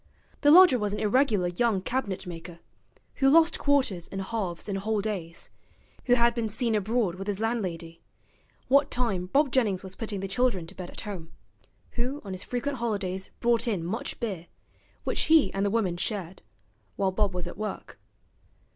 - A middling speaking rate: Yes, average, 180 wpm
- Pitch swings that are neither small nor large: Yes, average, 4.3 semitones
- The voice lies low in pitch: No, high, 210 Hz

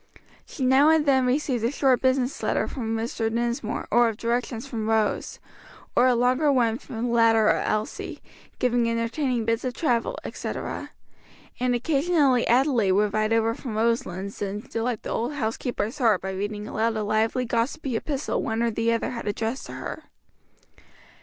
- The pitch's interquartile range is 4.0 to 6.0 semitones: No, narrow, 2.4 semitones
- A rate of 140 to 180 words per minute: Yes, average, 170 wpm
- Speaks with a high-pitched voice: Yes, high, 235 Hz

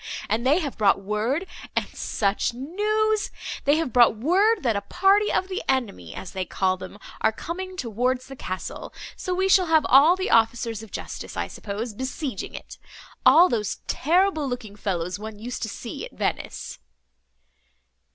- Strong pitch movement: Yes, wide, 8.9 semitones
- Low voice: No, very high, 255 Hz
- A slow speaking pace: No, average, 165 wpm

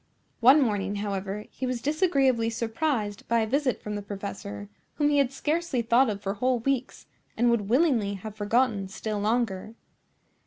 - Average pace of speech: Yes, average, 165 wpm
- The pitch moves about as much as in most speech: Yes, average, 4.3 semitones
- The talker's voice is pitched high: Yes, high, 230 Hz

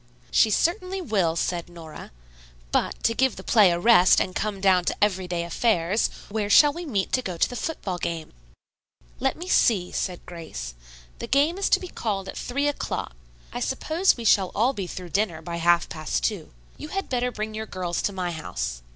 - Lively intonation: Yes, wide, 6.1 semitones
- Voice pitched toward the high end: Yes, high, 195 Hz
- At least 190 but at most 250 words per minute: Yes, average, 200 wpm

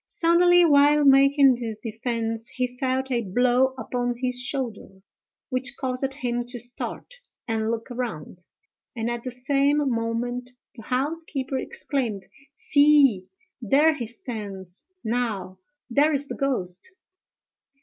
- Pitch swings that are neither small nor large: Yes, average, 3.3 semitones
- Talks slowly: Yes, slow, 120 wpm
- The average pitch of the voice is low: No, very high, 250 Hz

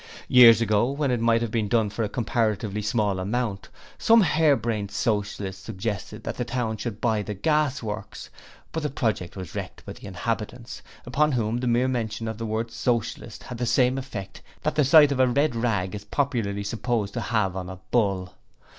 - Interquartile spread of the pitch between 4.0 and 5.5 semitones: No, average, 3.2 semitones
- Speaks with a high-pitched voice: No, low, 115 Hz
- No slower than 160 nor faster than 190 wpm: No, average, 200 wpm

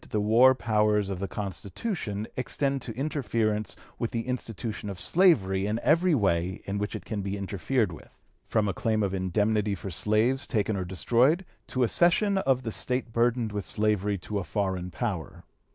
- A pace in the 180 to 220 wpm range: Yes, average, 185 wpm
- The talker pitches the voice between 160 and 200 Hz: No, low, 110 Hz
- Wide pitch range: No, average, 4.1 semitones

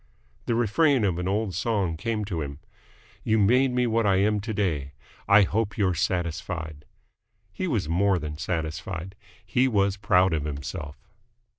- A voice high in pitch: No, very low, 95 Hz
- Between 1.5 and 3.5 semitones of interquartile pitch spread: No, average, 4.9 semitones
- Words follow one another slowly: No, average, 160 wpm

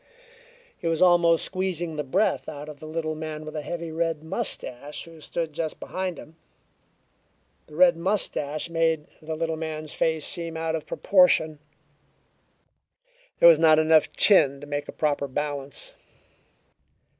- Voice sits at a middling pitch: Yes, medium, 160 Hz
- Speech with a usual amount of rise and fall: No, narrow, 1.7 semitones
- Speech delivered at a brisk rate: No, average, 155 wpm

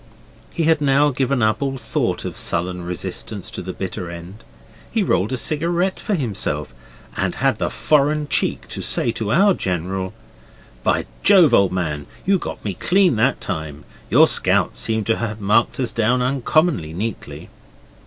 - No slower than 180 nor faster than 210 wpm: No, average, 165 wpm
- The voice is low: Yes, low, 115 Hz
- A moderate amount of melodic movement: No, wide, 8.0 semitones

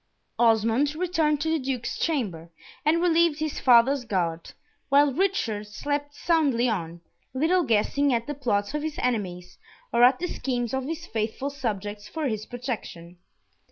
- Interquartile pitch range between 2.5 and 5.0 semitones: No, wide, 5.6 semitones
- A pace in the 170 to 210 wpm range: No, average, 155 wpm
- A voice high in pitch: Yes, very high, 255 Hz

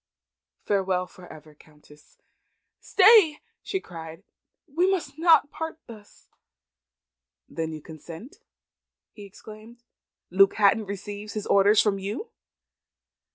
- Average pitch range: No, wide, 7.3 semitones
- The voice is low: No, high, 205 Hz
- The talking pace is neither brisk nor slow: No, slow, 110 wpm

